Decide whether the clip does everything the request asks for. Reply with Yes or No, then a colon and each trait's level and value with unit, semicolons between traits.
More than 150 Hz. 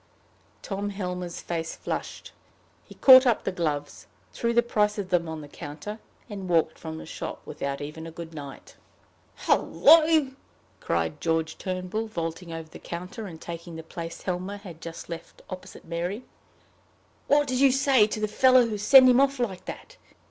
Yes: medium, 185 Hz